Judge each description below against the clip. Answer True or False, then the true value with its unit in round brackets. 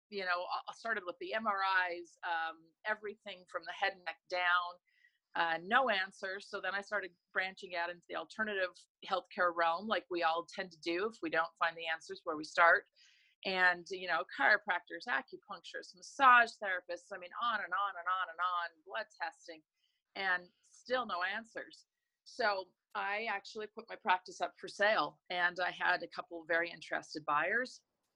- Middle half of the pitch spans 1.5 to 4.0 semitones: True (3.0 semitones)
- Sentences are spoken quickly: False (180 wpm)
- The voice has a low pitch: False (185 Hz)